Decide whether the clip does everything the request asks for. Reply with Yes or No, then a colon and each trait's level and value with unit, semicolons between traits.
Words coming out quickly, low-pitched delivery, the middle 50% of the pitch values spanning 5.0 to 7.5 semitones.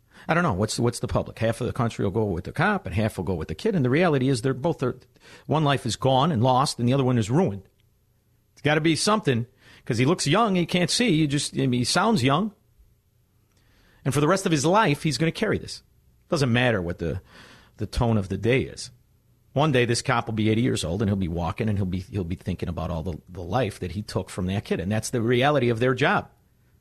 Yes: fast, 270 wpm; low, 120 Hz; average, 5.3 semitones